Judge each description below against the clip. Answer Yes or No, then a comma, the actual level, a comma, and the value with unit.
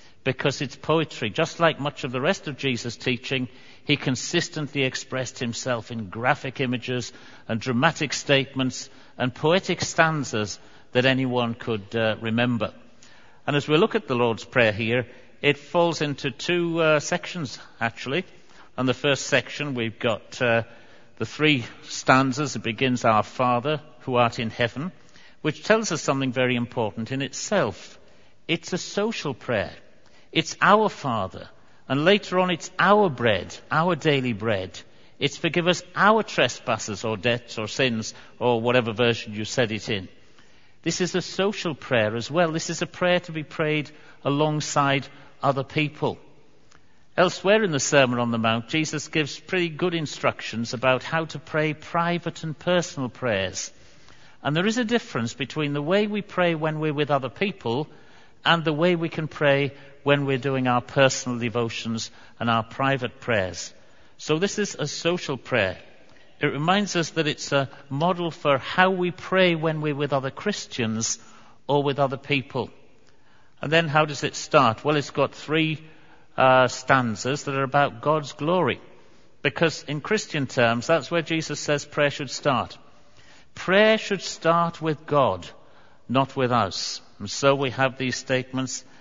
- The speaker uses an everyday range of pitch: Yes, average, 4.5 semitones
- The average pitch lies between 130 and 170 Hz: Yes, medium, 140 Hz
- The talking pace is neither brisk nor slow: Yes, average, 160 wpm